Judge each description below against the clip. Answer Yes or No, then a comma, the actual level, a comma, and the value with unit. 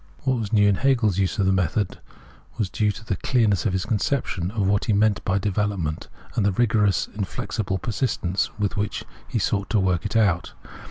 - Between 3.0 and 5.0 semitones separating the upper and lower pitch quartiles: No, narrow, 2.5 semitones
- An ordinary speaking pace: No, fast, 210 wpm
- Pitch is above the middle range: No, low, 100 Hz